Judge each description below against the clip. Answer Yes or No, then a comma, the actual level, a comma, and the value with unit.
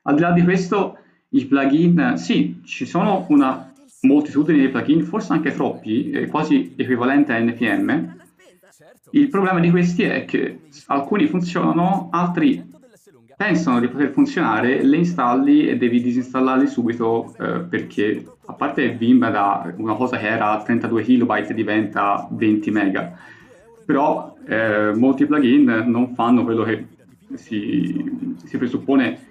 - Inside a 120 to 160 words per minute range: Yes, average, 135 wpm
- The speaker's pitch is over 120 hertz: Yes, medium, 140 Hz